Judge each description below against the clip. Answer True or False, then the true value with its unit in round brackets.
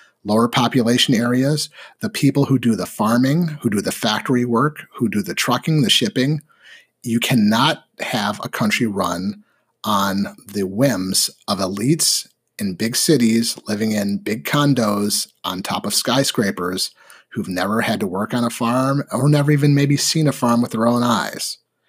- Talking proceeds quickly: False (165 wpm)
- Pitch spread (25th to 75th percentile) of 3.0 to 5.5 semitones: True (4.3 semitones)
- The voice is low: True (125 Hz)